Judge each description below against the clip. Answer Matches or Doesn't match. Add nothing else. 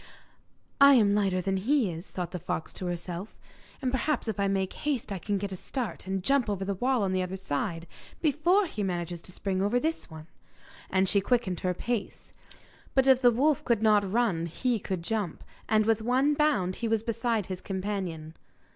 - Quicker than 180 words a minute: Matches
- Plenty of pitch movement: Doesn't match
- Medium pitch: Doesn't match